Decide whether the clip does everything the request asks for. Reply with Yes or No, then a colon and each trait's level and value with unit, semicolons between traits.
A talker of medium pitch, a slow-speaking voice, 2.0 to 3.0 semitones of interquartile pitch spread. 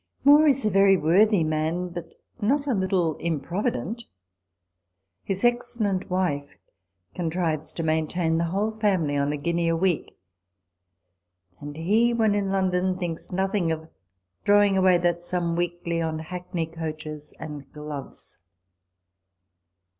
No: medium, 175 Hz; slow, 130 wpm; average, 3.5 semitones